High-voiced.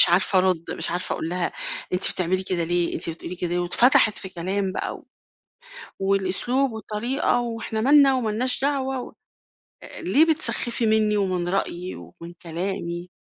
Yes: high, 195 Hz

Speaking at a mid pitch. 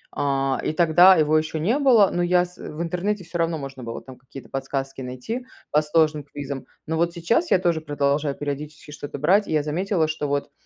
Yes: medium, 155 Hz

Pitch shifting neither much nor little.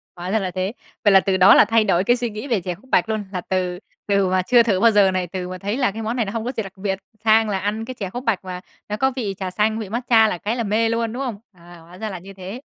Yes: average, 3.3 semitones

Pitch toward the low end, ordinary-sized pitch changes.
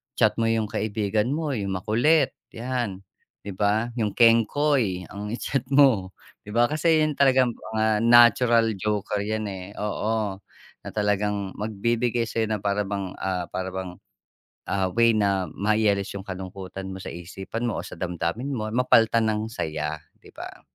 Yes: low, 105 Hz; average, 3.3 semitones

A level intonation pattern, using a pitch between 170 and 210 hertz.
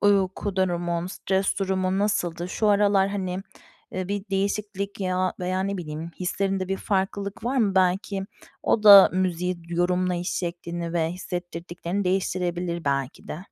Yes: narrow, 2.0 semitones; medium, 185 Hz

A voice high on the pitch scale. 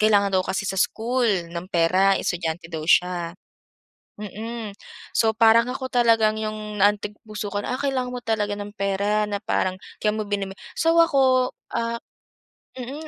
Yes: high, 210 Hz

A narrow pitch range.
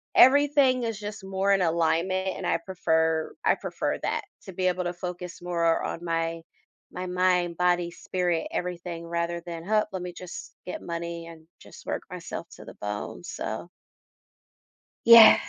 Yes: narrow, 2.0 semitones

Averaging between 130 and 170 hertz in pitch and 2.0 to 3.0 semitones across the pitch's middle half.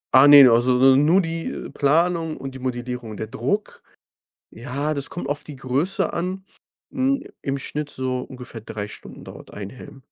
No: low, 135 Hz; average, 4.5 semitones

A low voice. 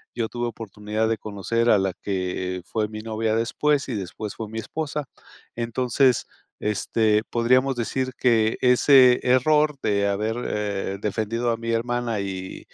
Yes: low, 115 Hz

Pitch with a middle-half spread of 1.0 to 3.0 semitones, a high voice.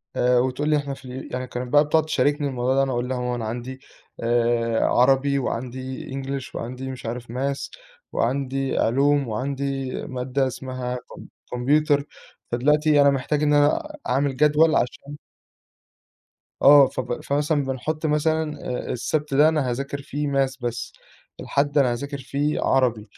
No: narrow, 2.5 semitones; low, 135 Hz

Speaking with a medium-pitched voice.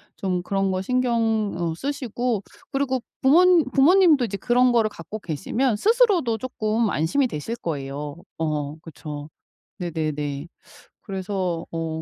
No: high, 205 Hz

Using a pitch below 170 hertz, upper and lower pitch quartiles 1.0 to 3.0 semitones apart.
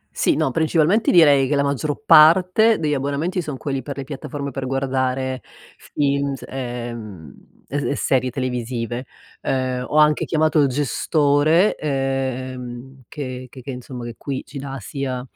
Yes: low, 135 Hz; narrow, 2.5 semitones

